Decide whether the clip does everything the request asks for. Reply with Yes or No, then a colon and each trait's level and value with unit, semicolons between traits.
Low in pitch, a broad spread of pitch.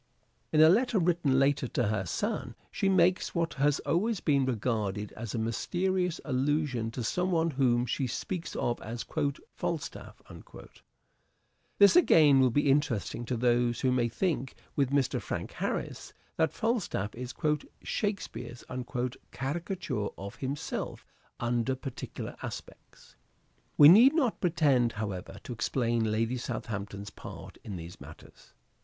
Yes: low, 130 Hz; wide, 6.1 semitones